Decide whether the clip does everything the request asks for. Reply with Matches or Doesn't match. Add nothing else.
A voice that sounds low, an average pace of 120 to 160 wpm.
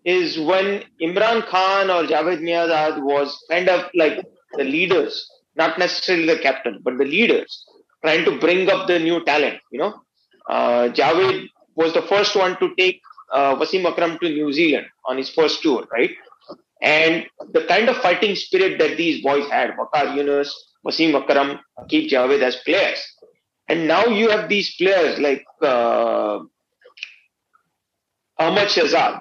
Doesn't match